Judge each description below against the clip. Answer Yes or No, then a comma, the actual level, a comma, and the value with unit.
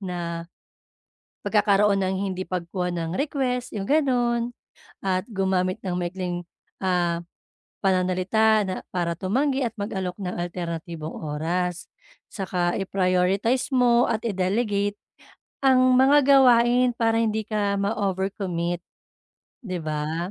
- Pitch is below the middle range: No, high, 190 Hz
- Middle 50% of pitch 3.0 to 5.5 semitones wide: Yes, average, 4.1 semitones